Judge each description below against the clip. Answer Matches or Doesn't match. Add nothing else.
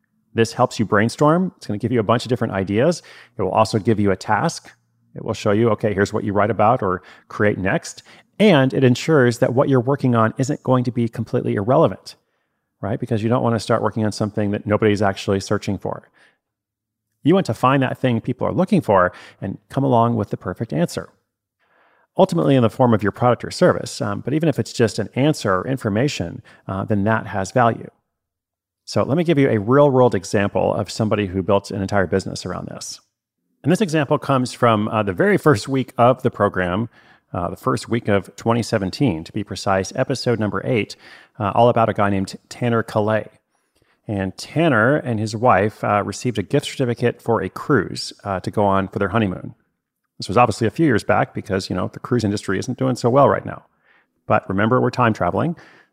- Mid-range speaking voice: Doesn't match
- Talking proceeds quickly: Matches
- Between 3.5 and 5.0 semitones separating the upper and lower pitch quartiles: Matches